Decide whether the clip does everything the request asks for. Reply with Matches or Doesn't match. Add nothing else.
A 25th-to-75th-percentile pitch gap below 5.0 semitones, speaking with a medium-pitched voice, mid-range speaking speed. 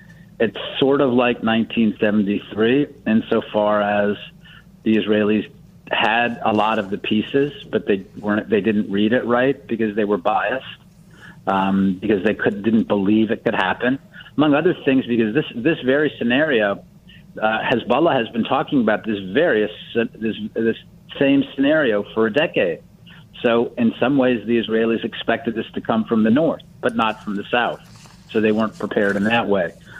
Doesn't match